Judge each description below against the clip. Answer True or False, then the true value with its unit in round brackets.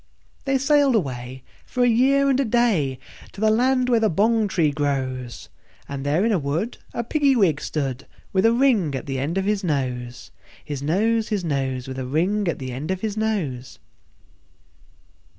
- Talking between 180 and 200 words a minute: True (185 wpm)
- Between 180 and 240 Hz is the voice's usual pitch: True (185 Hz)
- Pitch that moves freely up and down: True (8.8 semitones)